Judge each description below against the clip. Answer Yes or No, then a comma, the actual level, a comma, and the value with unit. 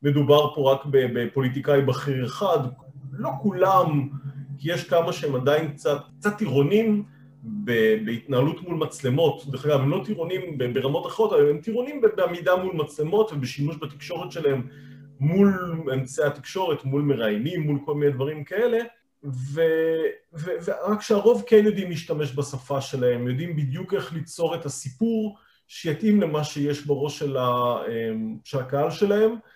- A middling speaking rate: Yes, average, 140 wpm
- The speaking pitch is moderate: Yes, medium, 145 Hz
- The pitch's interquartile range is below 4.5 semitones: No, average, 5.0 semitones